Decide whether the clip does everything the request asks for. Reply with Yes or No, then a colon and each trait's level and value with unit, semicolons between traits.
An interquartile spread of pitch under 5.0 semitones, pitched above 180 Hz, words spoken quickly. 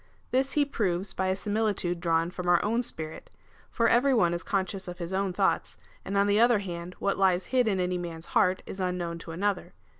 Yes: average, 3.0 semitones; high, 190 Hz; fast, 215 wpm